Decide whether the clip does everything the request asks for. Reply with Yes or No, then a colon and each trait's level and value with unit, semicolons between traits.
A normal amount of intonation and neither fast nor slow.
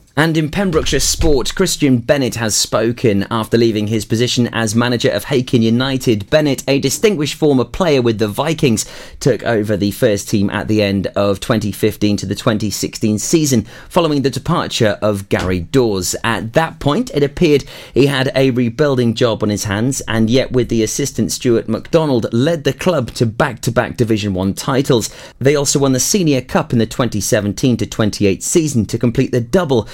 Yes: average, 4.4 semitones; average, 180 wpm